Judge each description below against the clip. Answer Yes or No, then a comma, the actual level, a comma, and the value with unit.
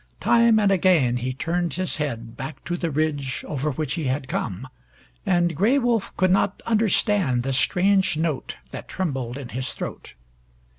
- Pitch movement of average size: No, wide, 6.1 semitones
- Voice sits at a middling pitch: Yes, medium, 155 Hz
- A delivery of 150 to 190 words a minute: Yes, average, 165 wpm